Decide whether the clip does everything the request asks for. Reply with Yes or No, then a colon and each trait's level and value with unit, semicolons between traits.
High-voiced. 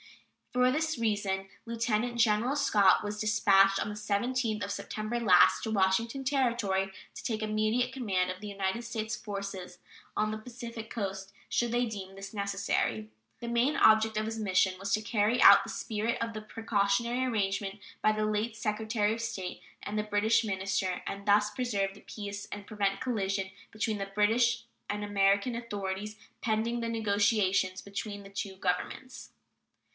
Yes: high, 210 Hz